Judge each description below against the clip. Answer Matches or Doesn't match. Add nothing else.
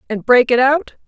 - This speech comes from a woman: Matches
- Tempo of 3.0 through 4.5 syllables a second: Doesn't match